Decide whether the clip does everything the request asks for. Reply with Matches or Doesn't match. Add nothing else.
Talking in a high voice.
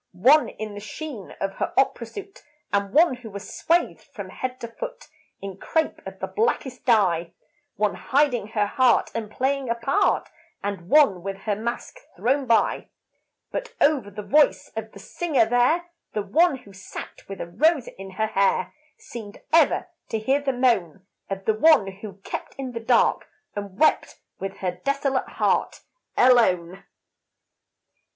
Matches